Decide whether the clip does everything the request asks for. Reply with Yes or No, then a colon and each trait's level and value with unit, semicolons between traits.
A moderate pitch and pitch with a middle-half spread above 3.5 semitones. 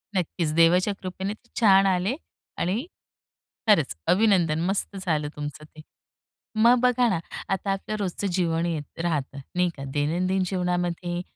No: medium, 180 Hz; average, 3.1 semitones